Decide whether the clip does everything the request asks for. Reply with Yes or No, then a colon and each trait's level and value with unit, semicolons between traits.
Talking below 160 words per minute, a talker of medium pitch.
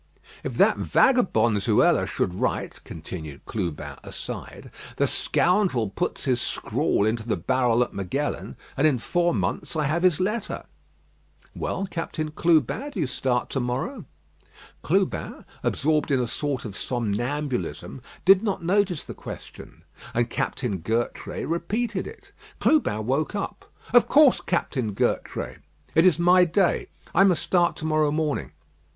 Yes: average, 145 wpm; medium, 150 Hz